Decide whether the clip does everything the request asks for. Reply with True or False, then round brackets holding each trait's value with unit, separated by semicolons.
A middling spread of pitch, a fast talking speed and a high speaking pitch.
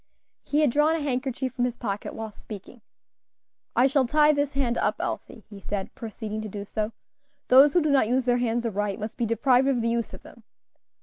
True (3.9 semitones; 210 wpm; 240 Hz)